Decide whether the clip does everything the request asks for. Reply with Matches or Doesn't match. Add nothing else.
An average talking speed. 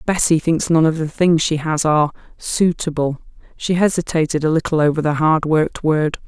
Matches